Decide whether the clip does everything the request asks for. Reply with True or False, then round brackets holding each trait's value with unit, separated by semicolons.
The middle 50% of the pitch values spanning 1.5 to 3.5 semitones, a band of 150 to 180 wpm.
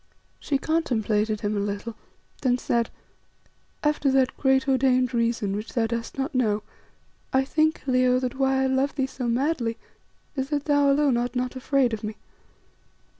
True (2.8 semitones; 165 wpm)